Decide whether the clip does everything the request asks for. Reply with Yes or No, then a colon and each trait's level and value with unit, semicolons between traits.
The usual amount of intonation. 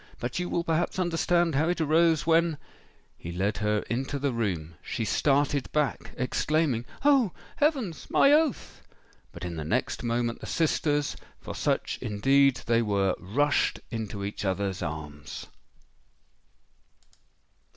No: wide, 8.1 semitones